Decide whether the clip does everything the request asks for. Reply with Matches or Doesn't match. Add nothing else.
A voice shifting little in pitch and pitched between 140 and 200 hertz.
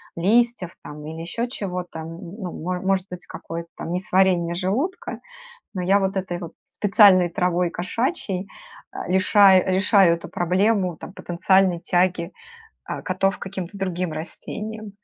Matches